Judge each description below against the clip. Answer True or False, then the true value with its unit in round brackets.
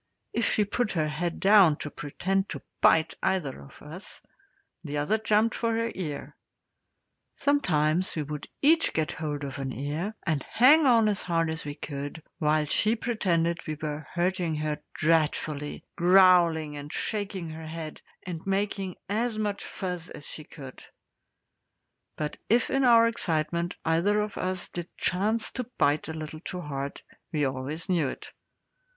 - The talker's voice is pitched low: False (170 Hz)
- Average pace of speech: True (160 wpm)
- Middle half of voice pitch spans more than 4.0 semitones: True (5.1 semitones)